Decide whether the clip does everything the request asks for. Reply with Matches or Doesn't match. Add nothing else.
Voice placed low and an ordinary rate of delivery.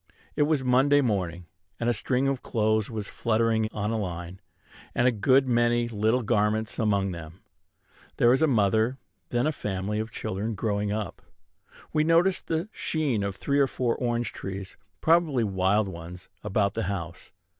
Matches